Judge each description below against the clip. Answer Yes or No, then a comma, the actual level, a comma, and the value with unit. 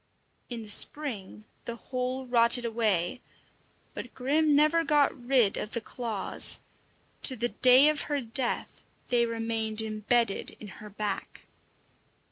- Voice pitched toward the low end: No, high, 235 Hz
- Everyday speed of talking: No, slow, 130 wpm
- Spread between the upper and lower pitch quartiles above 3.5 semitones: No, average, 3.2 semitones